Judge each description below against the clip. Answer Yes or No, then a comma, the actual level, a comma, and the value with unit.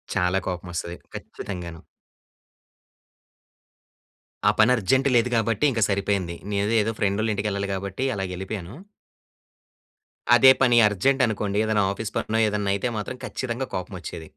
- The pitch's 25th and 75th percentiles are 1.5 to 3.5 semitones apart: Yes, average, 2.9 semitones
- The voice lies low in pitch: Yes, low, 105 Hz